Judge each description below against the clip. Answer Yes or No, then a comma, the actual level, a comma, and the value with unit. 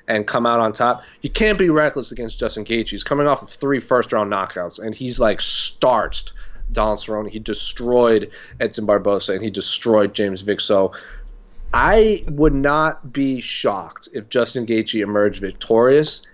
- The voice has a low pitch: Yes, low, 115 Hz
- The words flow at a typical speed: Yes, average, 165 wpm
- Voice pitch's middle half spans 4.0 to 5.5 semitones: Yes, average, 4.6 semitones